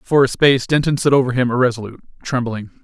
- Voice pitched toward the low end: Yes, low, 125 Hz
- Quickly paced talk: No, average, 190 wpm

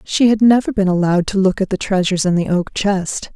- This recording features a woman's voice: Yes, female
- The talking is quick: Yes, fast, 250 wpm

